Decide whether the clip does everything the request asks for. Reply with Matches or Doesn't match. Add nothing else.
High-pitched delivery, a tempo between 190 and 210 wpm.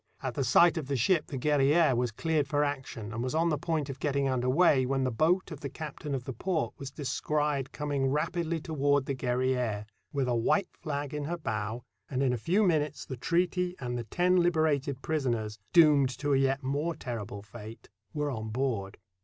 Doesn't match